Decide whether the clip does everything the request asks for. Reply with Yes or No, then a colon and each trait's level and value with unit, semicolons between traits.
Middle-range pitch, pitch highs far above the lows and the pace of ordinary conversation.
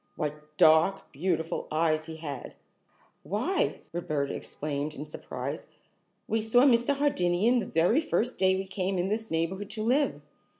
Yes: medium, 180 Hz; wide, 6.1 semitones; average, 145 wpm